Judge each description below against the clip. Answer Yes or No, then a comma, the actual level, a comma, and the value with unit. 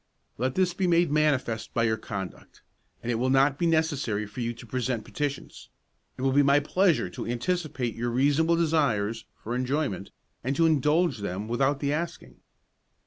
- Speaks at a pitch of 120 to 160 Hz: Yes, low, 135 Hz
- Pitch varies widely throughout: No, average, 4.8 semitones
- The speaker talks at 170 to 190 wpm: Yes, average, 175 wpm